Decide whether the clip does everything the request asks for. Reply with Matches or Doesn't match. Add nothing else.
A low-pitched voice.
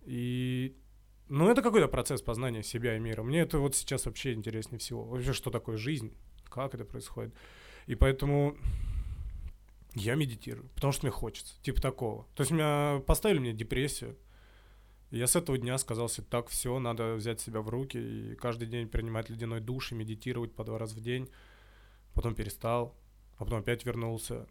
Matches